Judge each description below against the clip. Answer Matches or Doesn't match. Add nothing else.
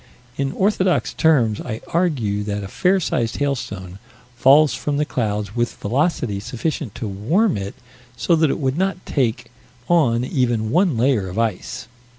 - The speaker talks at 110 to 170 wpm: Matches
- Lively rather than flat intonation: Matches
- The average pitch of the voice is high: Doesn't match